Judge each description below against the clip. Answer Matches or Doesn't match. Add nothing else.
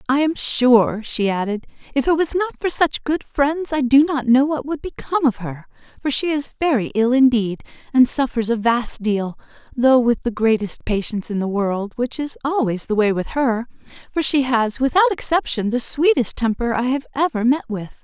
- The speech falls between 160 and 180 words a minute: Doesn't match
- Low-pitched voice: Doesn't match